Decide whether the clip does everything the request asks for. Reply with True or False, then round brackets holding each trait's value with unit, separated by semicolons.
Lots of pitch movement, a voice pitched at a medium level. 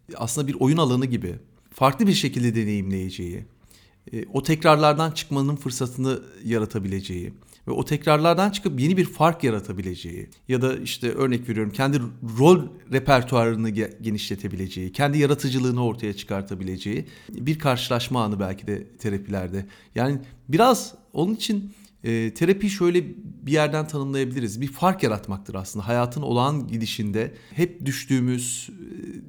False (5.7 semitones; 125 Hz)